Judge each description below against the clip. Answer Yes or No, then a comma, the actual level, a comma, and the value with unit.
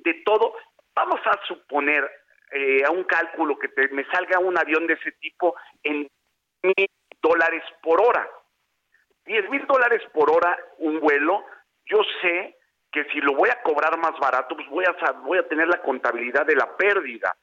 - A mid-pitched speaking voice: Yes, medium, 165 Hz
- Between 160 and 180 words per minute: Yes, average, 170 wpm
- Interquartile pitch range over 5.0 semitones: No, average, 4.1 semitones